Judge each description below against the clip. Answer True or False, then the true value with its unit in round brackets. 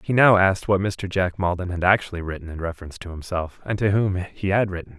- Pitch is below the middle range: True (95 Hz)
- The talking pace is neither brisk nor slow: False (240 wpm)